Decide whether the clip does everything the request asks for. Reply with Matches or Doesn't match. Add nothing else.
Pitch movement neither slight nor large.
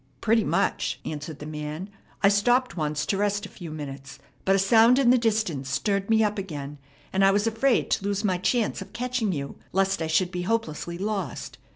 Doesn't match